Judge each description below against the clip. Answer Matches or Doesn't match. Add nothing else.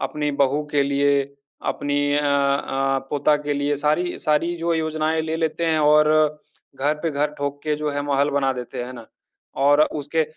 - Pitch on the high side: Doesn't match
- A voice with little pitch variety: Matches